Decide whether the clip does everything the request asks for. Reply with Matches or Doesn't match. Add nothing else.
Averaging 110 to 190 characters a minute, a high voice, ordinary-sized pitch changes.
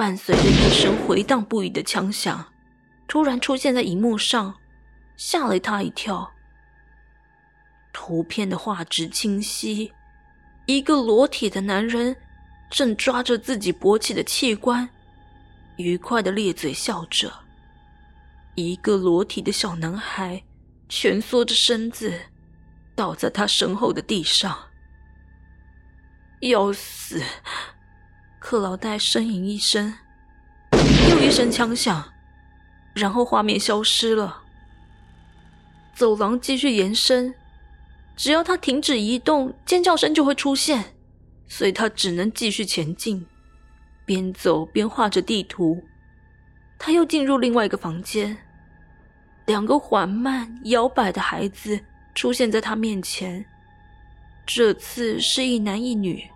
Doesn't match